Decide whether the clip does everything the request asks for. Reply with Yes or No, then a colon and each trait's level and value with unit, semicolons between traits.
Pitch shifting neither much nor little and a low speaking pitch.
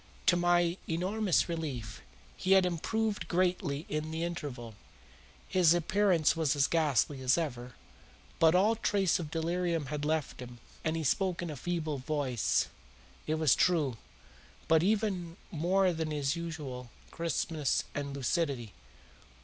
No: average, 3.6 semitones; medium, 160 Hz